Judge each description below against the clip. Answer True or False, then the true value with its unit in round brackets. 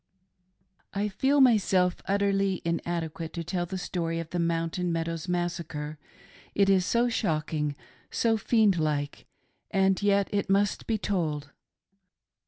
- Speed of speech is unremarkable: False (130 wpm)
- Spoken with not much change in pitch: False (3.3 semitones)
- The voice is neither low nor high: True (180 Hz)